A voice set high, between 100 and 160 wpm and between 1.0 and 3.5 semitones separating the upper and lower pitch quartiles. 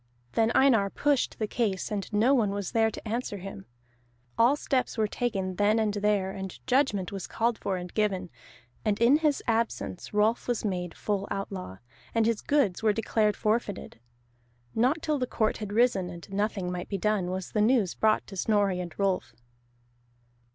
No: high, 210 Hz; average, 180 wpm; average, 3.2 semitones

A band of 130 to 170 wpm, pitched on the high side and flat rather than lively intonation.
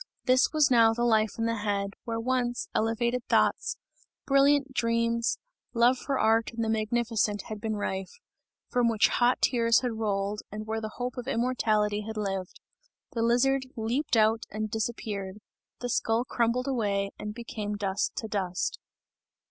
Yes: average, 160 wpm; high, 225 Hz; narrow, 2.3 semitones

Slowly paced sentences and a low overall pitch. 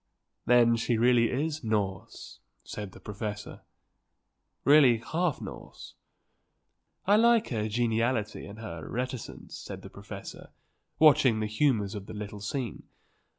Yes: slow, 125 wpm; low, 115 Hz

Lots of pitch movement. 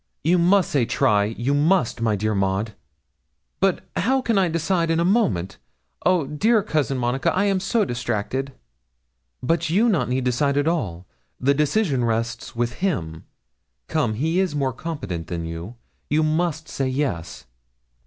Yes: wide, 7.1 semitones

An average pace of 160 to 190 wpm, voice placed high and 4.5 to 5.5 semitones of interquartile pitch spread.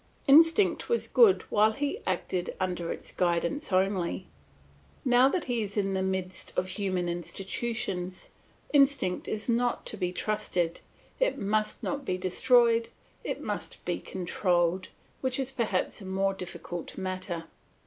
No: average, 140 wpm; high, 195 Hz; average, 5.1 semitones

